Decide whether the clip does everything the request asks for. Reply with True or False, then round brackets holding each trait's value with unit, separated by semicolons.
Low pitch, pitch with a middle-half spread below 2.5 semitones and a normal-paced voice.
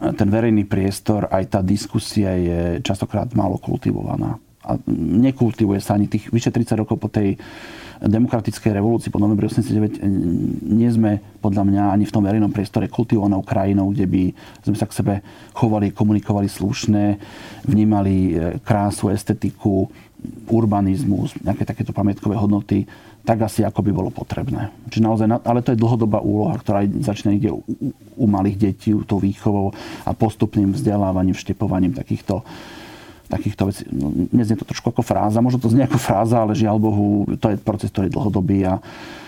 True (105 Hz; 2.1 semitones; 155 wpm)